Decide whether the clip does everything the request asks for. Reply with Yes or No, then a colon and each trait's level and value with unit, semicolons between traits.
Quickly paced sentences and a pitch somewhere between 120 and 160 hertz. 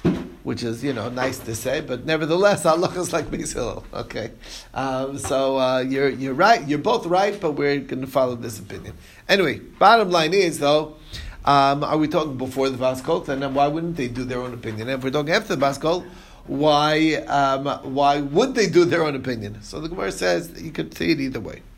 Yes: fast, 220 wpm; medium, 140 Hz